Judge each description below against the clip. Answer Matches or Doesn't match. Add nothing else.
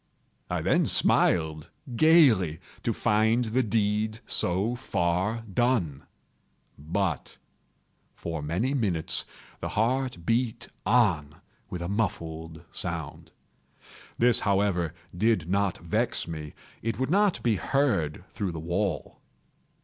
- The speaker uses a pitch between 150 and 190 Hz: Doesn't match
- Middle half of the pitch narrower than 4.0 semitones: Doesn't match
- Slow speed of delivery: Matches